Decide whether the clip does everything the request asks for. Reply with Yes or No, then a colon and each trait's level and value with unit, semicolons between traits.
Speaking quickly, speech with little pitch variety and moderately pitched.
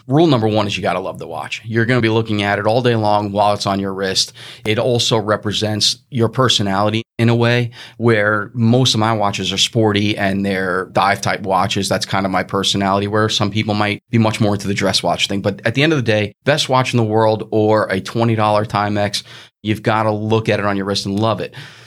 No: fast, 240 wpm; narrow, 2.2 semitones; low, 110 Hz